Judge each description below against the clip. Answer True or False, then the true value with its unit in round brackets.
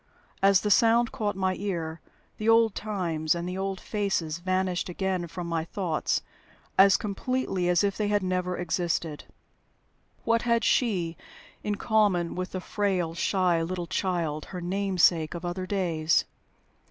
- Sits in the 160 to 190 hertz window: True (185 Hz)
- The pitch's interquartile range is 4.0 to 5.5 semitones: False (2.9 semitones)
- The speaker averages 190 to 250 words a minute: False (150 wpm)